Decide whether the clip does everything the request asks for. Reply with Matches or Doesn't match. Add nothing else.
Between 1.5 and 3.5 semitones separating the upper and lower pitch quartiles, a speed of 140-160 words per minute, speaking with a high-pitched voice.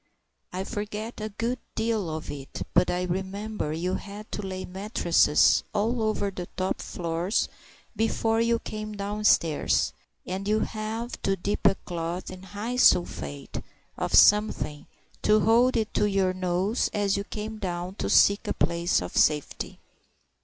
Matches